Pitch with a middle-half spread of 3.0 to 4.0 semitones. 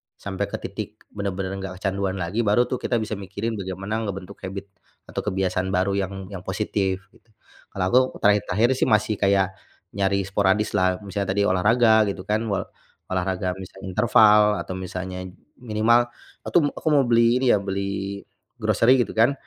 No: narrow, 2.4 semitones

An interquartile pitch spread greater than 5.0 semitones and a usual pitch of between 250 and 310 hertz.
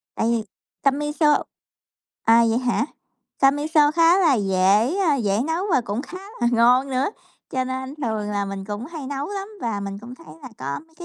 Yes: wide, 5.5 semitones; very high, 255 Hz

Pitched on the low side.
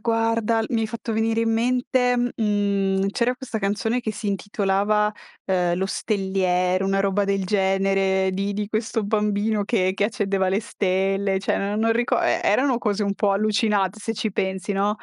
No: high, 205 Hz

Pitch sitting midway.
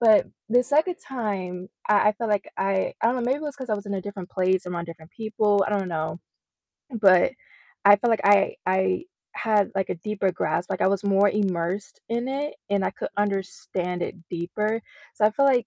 No: high, 200 Hz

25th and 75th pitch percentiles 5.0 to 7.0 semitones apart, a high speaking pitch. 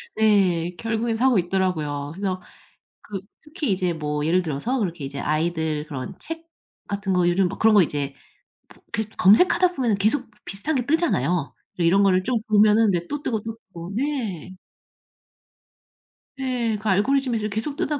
Yes: wide, 5.4 semitones; high, 200 Hz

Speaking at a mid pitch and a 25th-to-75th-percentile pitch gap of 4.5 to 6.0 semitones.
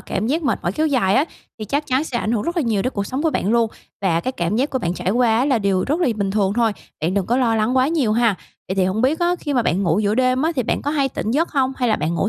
No: high, 235 Hz; average, 5.1 semitones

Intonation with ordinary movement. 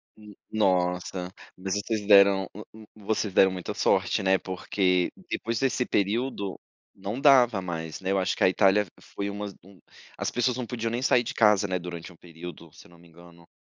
Yes: average, 3.2 semitones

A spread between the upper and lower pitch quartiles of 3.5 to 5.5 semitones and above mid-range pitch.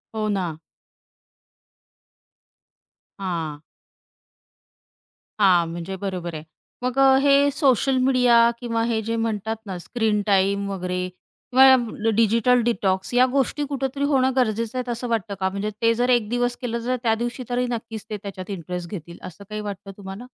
Yes: average, 4.2 semitones; high, 220 Hz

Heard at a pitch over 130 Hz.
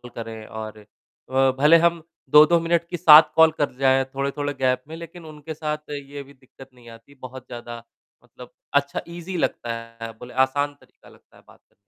Yes: medium, 140 Hz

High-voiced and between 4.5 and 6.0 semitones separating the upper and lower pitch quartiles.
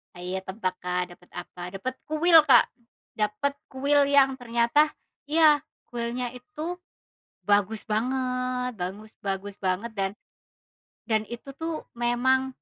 Yes: high, 240 Hz; average, 4.9 semitones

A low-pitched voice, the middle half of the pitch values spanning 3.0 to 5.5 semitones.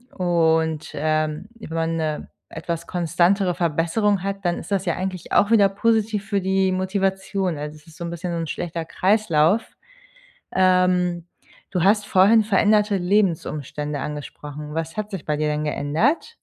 No: medium, 180 Hz; average, 3.6 semitones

